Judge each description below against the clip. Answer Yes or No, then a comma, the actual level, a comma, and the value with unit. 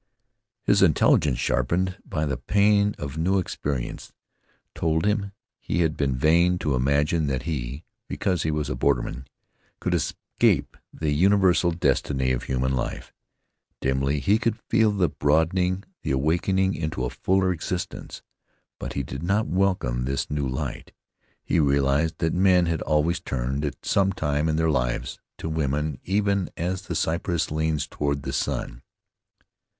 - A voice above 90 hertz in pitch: No, very low, 80 Hz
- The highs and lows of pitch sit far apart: No, average, 4.8 semitones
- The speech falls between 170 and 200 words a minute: No, average, 150 wpm